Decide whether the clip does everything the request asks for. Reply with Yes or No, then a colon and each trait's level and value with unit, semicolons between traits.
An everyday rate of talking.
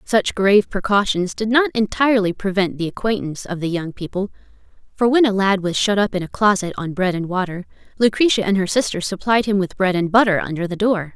No: fast, 215 wpm